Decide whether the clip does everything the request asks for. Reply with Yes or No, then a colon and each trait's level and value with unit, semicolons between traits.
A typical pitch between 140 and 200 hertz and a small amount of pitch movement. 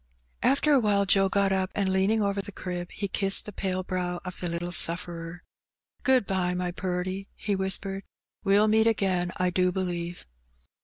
Yes: high, 190 Hz; narrow, 1.9 semitones